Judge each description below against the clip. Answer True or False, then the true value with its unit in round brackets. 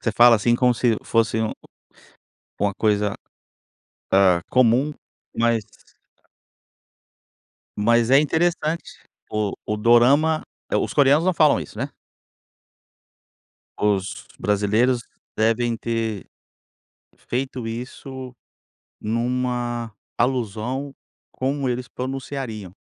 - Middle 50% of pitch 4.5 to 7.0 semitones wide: False (3.2 semitones)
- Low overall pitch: True (120 Hz)